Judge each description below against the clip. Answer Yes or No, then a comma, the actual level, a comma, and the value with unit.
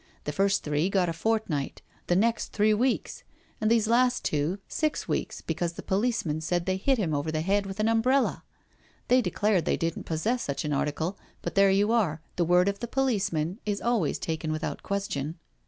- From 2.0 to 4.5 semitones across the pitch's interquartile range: No, wide, 5.5 semitones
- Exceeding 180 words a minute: Yes, average, 195 wpm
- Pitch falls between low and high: No, high, 195 Hz